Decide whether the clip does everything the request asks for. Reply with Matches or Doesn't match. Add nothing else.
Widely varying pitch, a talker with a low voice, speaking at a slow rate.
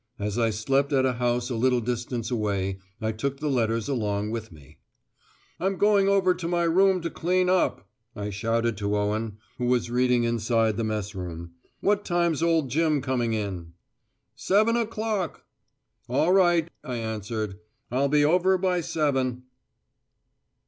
Doesn't match